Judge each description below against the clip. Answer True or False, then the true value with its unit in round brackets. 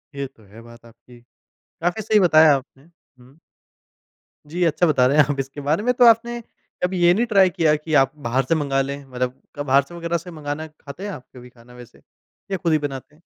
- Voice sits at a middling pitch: True (150 Hz)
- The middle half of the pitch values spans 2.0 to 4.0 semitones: False (4.7 semitones)